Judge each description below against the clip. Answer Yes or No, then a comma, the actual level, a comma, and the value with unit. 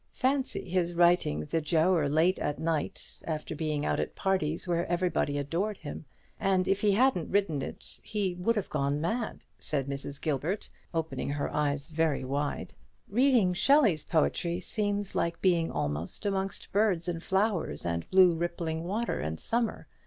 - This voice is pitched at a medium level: Yes, medium, 170 Hz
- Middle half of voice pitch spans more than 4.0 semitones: Yes, average, 4.5 semitones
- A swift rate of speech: No, average, 155 wpm